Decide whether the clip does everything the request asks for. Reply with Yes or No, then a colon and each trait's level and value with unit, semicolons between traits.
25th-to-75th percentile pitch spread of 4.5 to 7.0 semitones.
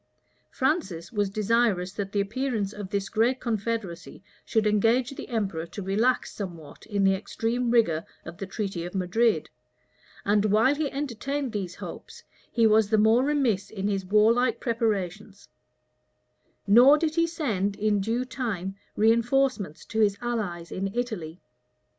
No: average, 3.6 semitones